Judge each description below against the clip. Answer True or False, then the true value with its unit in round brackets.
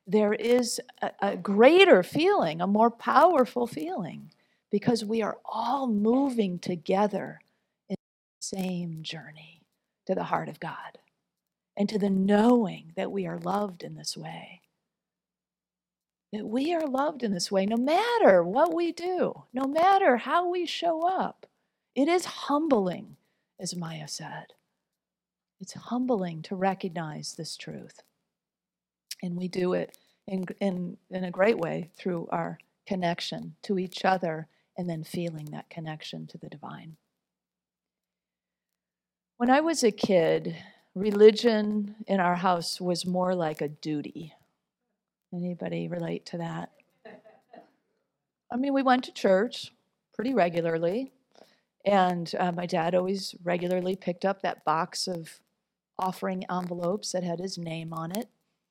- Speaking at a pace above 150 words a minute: False (140 wpm)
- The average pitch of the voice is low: False (195 Hz)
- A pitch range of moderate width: True (4.9 semitones)